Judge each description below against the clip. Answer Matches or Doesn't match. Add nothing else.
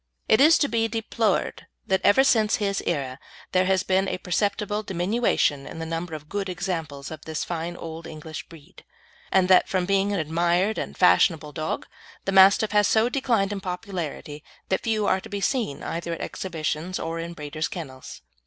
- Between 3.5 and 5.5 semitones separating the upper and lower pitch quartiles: Matches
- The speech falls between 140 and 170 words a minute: Doesn't match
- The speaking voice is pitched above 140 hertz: Matches